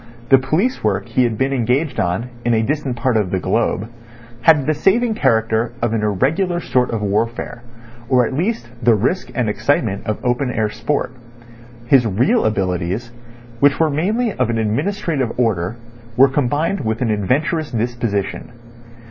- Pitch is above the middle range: No, low, 120 Hz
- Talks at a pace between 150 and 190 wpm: Yes, average, 165 wpm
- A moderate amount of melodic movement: Yes, average, 4.9 semitones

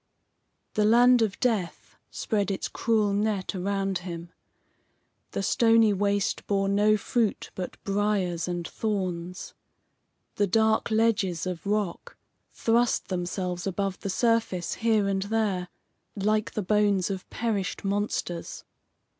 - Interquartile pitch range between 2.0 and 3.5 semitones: Yes, average, 2.7 semitones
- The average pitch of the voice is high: Yes, high, 200 Hz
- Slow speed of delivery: Yes, slow, 120 wpm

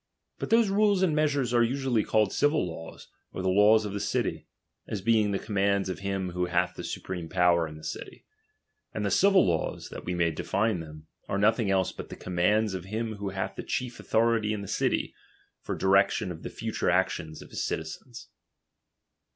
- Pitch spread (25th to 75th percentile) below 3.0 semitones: No, average, 4.0 semitones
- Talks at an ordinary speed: No, fast, 210 wpm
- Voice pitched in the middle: No, low, 100 Hz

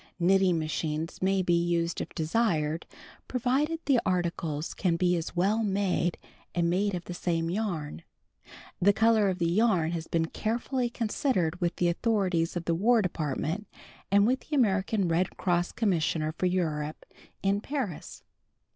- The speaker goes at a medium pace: Yes, average, 155 wpm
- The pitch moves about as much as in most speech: Yes, average, 3.9 semitones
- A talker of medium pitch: Yes, medium, 180 Hz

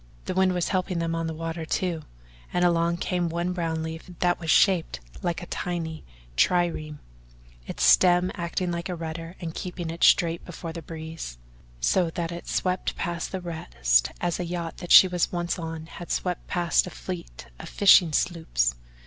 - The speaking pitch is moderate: Yes, medium, 170 Hz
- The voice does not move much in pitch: Yes, narrow, 1.6 semitones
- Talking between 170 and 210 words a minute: Yes, average, 185 wpm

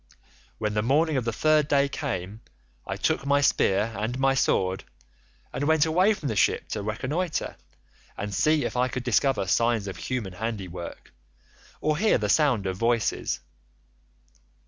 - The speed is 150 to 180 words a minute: Yes, average, 160 wpm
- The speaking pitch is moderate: No, low, 125 Hz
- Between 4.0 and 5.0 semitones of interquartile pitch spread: No, wide, 5.6 semitones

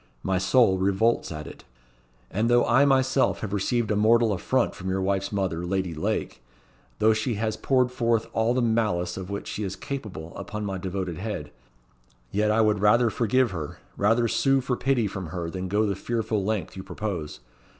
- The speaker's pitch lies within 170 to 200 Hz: No, low, 105 Hz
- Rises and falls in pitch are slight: No, average, 3.7 semitones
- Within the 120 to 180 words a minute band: No, average, 190 wpm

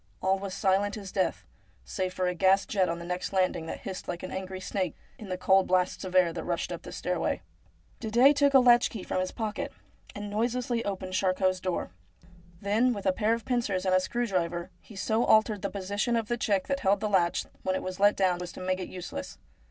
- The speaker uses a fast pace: Yes, fast, 230 wpm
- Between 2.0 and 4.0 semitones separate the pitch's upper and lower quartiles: Yes, average, 2.8 semitones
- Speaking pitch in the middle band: No, high, 195 Hz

